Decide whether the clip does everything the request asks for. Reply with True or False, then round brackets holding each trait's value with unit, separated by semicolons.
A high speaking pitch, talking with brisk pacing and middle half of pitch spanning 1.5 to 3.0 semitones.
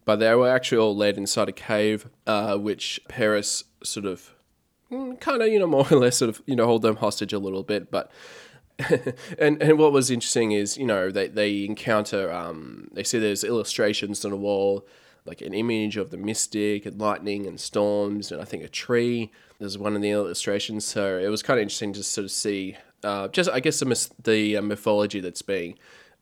False (105 Hz; 210 wpm; 2.4 semitones)